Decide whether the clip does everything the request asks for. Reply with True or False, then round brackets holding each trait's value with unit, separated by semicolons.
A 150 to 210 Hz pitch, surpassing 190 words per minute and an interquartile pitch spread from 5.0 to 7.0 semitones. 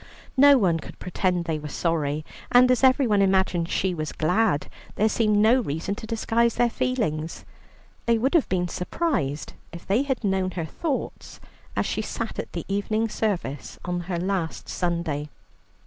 False (190 Hz; 165 wpm; 5.4 semitones)